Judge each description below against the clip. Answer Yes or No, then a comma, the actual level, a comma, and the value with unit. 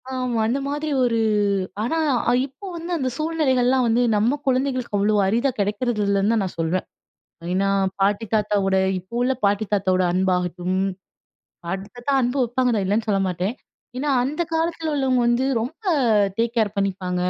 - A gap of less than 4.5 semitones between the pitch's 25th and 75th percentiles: No, average, 4.9 semitones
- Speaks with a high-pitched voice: Yes, high, 230 Hz